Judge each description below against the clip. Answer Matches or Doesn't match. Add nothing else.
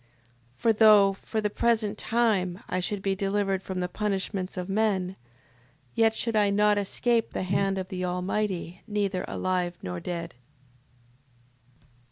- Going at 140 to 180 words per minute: Matches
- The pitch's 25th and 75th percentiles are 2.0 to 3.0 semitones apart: Matches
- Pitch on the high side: Matches